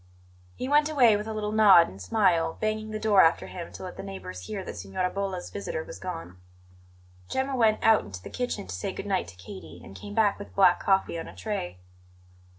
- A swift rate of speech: Yes, fast, 220 wpm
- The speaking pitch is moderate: No, high, 195 Hz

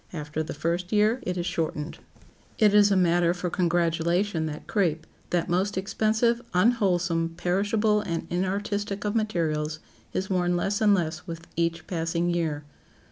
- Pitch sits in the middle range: Yes, medium, 175 Hz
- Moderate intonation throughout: Yes, average, 3.5 semitones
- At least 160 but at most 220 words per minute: No, average, 150 wpm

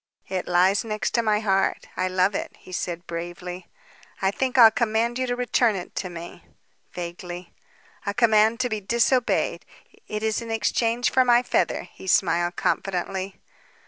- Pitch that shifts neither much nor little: Yes, average, 4.3 semitones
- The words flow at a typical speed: Yes, average, 160 wpm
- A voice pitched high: Yes, high, 205 Hz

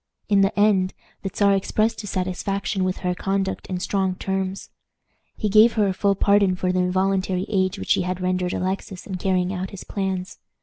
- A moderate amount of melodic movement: No, narrow, 1.3 semitones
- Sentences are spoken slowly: No, average, 190 wpm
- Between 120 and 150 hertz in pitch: No, high, 190 Hz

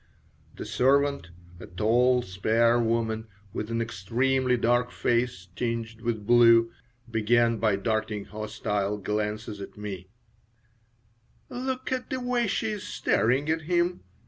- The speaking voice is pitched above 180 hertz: No, low, 115 Hz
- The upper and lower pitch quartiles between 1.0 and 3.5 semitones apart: Yes, average, 3.1 semitones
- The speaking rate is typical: No, slow, 125 wpm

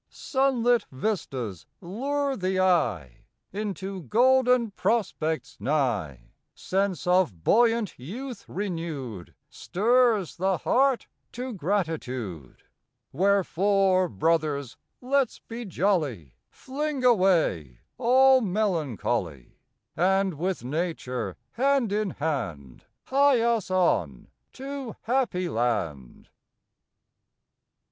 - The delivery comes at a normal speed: No, slow, 85 wpm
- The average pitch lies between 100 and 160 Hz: No, medium, 185 Hz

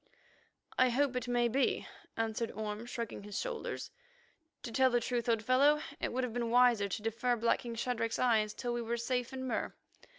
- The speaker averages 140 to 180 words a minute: No, average, 190 wpm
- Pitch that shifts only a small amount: Yes, narrow, 1.8 semitones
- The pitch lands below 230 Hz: No, high, 240 Hz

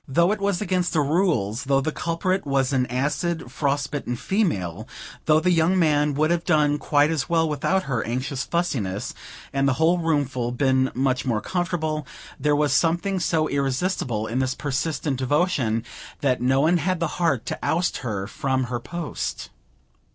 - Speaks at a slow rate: No, average, 175 wpm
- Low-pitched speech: No, medium, 145 Hz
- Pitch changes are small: No, average, 4.5 semitones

